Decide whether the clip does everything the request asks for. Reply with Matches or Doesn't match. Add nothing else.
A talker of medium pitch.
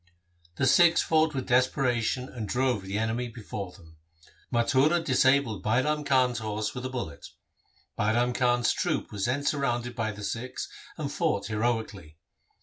Doesn't match